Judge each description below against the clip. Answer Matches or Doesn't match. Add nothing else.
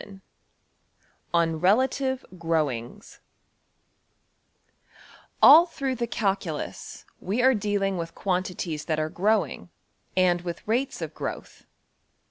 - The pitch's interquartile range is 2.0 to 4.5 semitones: Doesn't match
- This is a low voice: Doesn't match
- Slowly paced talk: Matches